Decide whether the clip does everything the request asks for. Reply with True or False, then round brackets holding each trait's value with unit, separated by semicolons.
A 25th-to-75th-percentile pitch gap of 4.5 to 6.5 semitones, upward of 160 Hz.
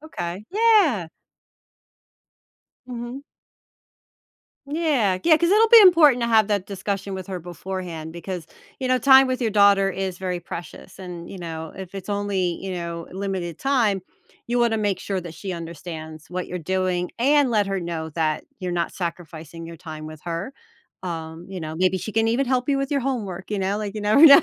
True (5.6 semitones; 190 Hz)